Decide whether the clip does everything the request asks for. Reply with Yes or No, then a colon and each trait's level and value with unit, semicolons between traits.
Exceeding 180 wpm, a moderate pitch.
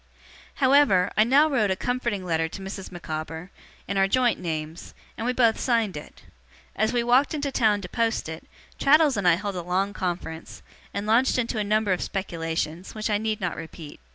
No: average, 195 wpm; high, 205 Hz